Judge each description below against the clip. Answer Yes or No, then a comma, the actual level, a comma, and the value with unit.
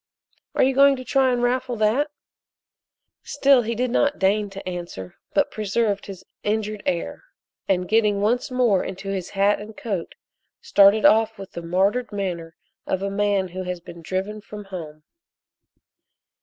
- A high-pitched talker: Yes, high, 205 Hz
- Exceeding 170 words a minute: No, average, 160 wpm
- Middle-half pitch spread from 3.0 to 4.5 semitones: Yes, average, 3.9 semitones